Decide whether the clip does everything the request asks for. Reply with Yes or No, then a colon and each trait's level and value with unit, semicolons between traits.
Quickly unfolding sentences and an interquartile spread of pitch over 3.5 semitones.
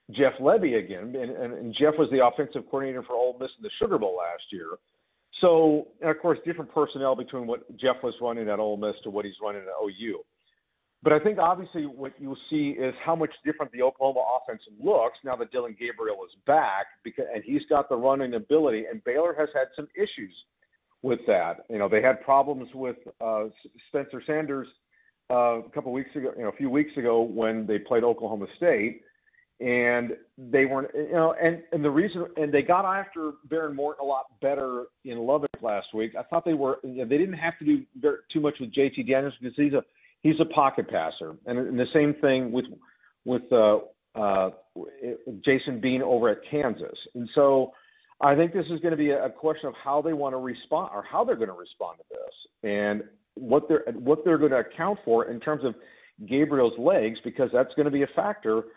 Yes: fast, 210 wpm; average, 4.6 semitones